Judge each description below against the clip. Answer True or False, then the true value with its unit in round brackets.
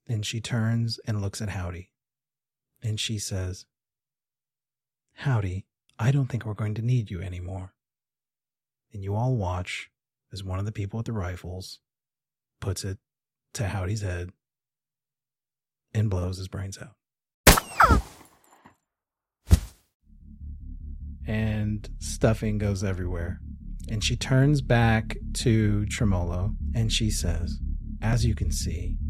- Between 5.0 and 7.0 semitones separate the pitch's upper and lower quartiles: True (5.5 semitones)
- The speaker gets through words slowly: True (120 wpm)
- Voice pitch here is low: True (110 Hz)